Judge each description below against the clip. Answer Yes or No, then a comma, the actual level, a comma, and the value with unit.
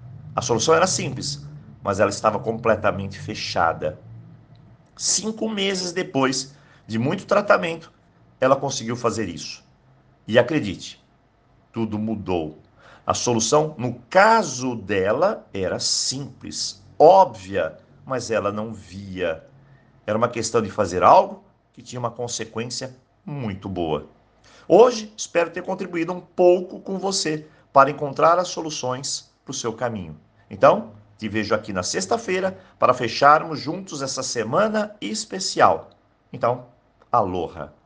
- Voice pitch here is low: Yes, low, 130 Hz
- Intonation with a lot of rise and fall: Yes, wide, 5.9 semitones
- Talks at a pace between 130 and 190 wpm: No, slow, 120 wpm